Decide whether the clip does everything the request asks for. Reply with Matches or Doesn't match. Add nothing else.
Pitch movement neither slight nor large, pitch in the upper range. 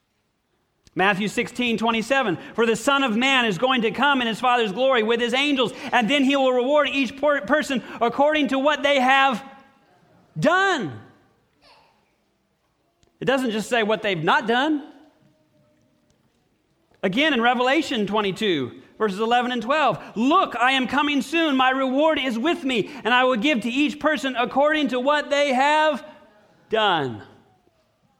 Matches